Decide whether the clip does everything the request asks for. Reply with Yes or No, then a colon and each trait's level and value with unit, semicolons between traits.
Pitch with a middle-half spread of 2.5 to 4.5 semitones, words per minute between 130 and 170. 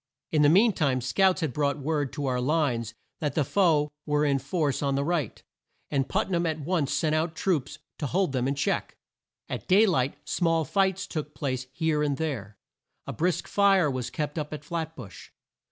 No: average, 3.5 semitones; average, 200 wpm